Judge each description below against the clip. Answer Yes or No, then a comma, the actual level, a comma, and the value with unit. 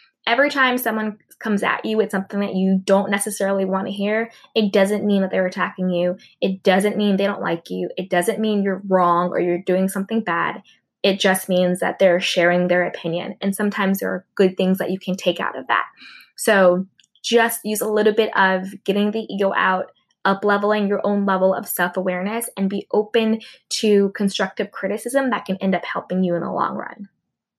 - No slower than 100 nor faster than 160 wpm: No, fast, 205 wpm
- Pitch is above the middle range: Yes, high, 195 Hz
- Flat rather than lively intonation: Yes, narrow, 2.2 semitones